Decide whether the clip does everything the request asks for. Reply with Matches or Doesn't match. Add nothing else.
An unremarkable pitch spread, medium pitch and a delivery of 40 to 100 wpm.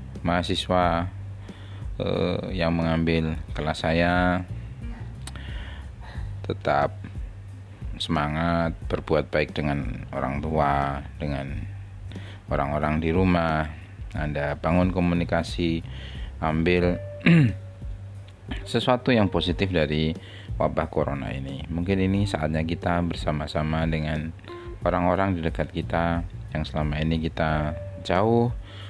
Doesn't match